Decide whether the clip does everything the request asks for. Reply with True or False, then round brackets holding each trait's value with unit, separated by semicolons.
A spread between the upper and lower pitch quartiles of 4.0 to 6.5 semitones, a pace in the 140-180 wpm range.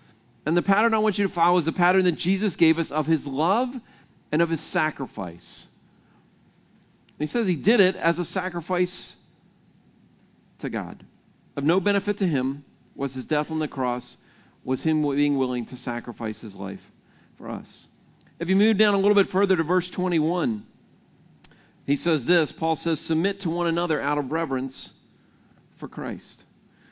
True (4.4 semitones; 175 wpm)